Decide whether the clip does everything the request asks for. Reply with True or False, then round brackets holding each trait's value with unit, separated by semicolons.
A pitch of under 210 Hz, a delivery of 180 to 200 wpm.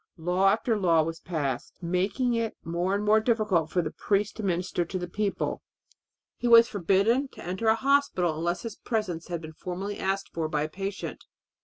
True (190 Hz; 190 wpm)